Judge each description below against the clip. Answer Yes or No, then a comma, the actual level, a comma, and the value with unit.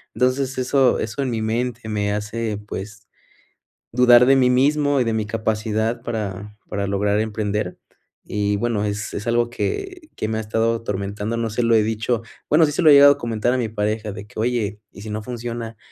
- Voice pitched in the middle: No, low, 110 Hz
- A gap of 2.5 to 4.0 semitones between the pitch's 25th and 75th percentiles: Yes, average, 2.9 semitones